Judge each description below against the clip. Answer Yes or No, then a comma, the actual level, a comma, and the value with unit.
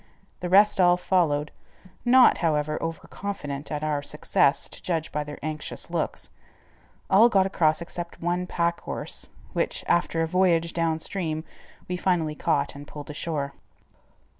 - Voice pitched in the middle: Yes, medium, 165 Hz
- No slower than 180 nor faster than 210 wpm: No, average, 150 wpm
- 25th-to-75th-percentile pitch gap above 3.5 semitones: No, average, 2.9 semitones